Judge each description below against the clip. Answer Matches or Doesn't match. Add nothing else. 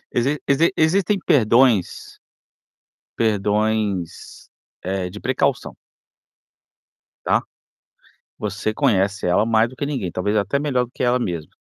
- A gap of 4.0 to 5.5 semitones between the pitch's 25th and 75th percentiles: Matches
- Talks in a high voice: Doesn't match